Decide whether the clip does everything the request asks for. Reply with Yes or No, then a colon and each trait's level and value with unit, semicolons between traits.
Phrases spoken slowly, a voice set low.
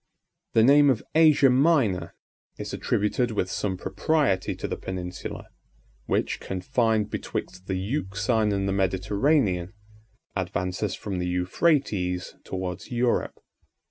Yes: slow, 115 wpm; low, 100 Hz